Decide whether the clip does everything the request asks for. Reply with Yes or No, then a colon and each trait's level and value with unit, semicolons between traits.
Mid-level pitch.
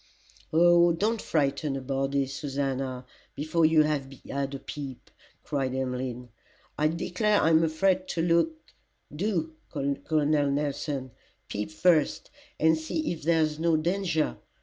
Yes: medium, 155 Hz